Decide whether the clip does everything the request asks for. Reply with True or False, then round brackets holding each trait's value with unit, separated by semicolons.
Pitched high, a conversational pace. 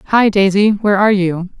True (200 Hz; 190 wpm)